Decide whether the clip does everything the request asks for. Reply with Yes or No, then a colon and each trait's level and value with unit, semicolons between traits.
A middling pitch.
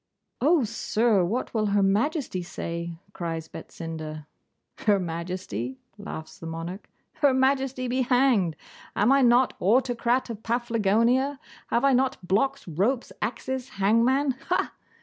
No: high, 230 Hz